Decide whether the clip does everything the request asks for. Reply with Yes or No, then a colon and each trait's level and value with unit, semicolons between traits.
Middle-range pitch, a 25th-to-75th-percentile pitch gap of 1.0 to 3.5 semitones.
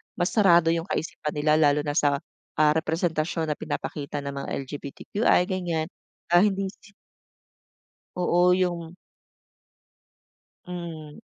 Yes: medium, 165 Hz; average, 2.9 semitones